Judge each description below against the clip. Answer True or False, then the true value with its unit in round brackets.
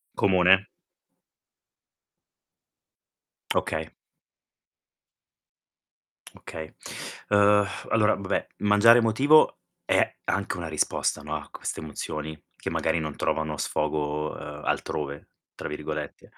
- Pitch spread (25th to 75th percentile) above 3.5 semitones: True (5.2 semitones)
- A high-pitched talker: False (85 Hz)